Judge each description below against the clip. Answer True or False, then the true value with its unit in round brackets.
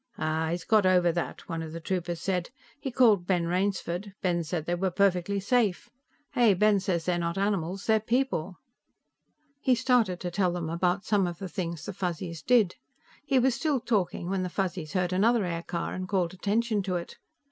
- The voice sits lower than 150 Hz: False (185 Hz)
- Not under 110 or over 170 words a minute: False (190 wpm)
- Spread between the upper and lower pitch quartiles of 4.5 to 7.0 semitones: False (3.2 semitones)